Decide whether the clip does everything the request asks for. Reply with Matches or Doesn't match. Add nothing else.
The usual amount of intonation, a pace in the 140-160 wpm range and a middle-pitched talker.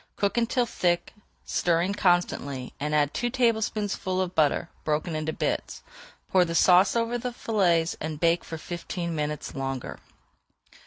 Matches